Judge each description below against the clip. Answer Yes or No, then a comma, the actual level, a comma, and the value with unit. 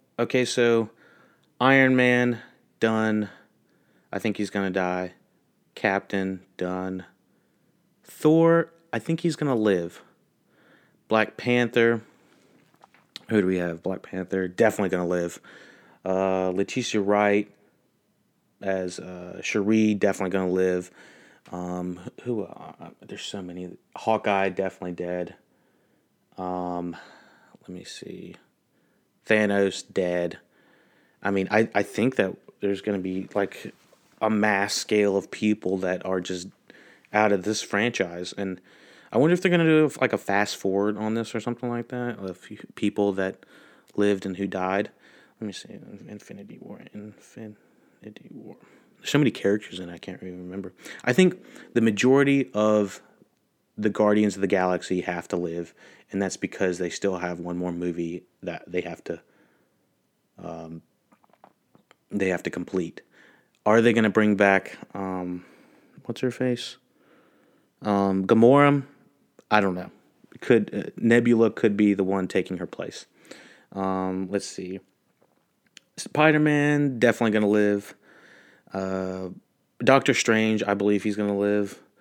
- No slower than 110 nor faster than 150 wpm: Yes, average, 140 wpm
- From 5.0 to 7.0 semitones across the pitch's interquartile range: No, average, 3.4 semitones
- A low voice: Yes, low, 100 Hz